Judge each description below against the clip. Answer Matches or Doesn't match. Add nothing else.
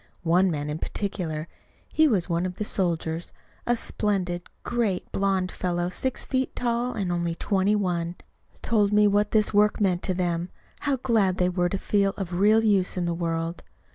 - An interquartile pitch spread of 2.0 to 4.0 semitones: Matches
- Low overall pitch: Doesn't match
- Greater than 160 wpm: Matches